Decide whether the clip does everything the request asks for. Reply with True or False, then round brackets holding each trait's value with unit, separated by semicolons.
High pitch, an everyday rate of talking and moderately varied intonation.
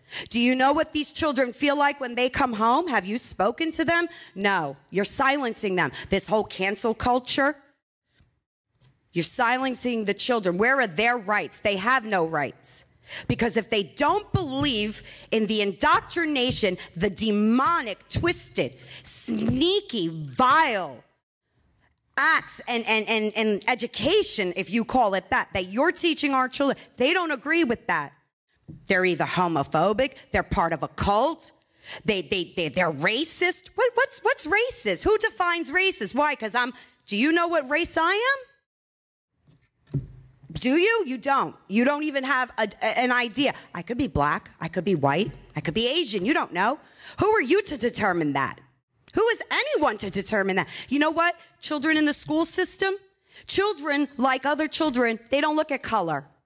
False (245 Hz; 165 wpm; 7.5 semitones)